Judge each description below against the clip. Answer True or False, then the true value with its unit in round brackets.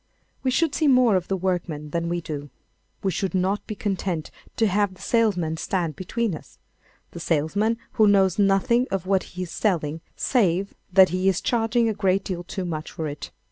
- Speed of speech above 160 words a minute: True (190 wpm)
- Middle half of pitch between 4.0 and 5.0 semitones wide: False (3.6 semitones)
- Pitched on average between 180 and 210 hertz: True (190 Hz)